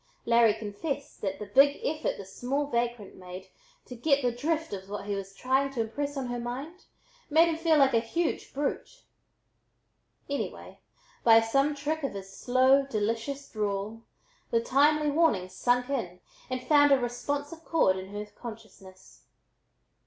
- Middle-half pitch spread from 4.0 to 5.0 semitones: No, wide, 5.4 semitones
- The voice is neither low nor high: No, high, 245 Hz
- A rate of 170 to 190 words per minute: No, average, 160 wpm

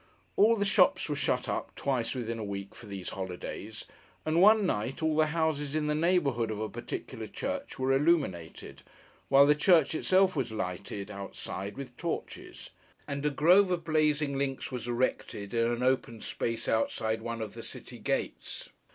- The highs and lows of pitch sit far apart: Yes, wide, 5.9 semitones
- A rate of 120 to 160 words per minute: No, average, 175 wpm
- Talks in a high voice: No, low, 135 Hz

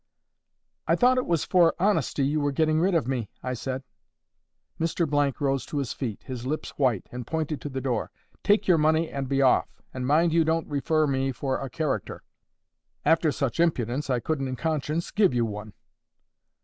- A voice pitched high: No, medium, 145 Hz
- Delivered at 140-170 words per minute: No, average, 190 wpm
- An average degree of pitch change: Yes, average, 3.8 semitones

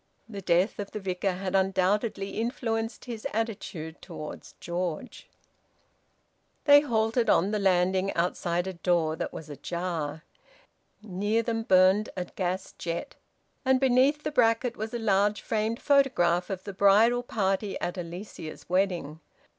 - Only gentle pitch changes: No, average, 4.1 semitones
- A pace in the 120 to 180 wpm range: Yes, average, 140 wpm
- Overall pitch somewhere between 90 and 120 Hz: No, high, 195 Hz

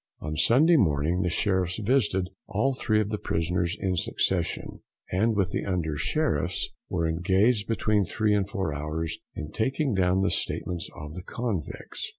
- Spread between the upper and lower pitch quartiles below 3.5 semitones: No, average, 4.3 semitones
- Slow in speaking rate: No, average, 160 wpm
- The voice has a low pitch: Yes, very low, 95 Hz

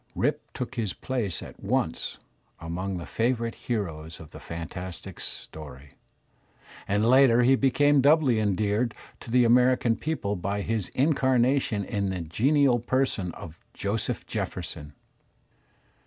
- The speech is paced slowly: Yes, slow, 125 wpm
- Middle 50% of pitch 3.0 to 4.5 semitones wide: No, wide, 5.6 semitones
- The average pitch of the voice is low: Yes, low, 110 Hz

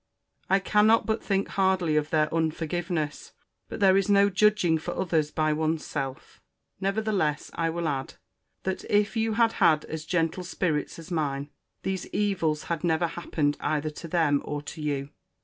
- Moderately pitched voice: Yes, medium, 165 Hz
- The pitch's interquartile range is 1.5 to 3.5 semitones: No, average, 4.0 semitones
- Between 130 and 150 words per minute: No, average, 165 wpm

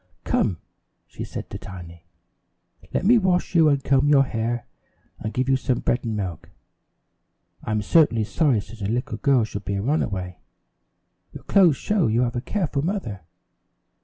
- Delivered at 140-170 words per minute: Yes, average, 165 wpm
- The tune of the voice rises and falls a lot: Yes, wide, 6.1 semitones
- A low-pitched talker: Yes, low, 120 Hz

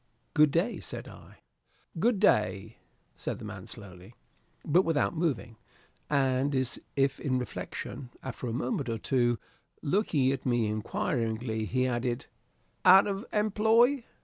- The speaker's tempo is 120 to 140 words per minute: Yes, slow, 135 wpm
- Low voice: Yes, low, 130 Hz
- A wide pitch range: Yes, wide, 6.9 semitones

